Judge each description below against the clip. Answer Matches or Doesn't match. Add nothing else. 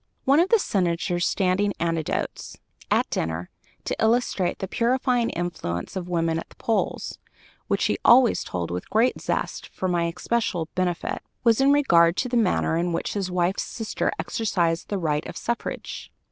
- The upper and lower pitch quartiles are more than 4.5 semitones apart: Matches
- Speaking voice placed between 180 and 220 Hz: Matches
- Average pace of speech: Matches